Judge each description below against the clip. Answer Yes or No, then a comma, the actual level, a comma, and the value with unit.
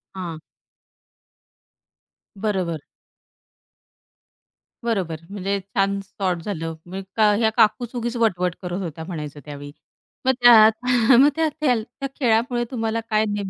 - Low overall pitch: No, high, 200 Hz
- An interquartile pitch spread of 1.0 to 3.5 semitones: No, average, 4.3 semitones